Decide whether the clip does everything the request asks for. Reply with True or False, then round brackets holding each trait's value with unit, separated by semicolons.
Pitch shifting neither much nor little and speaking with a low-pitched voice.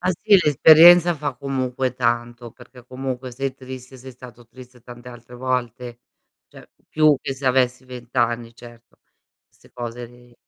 False (1.7 semitones; 125 Hz)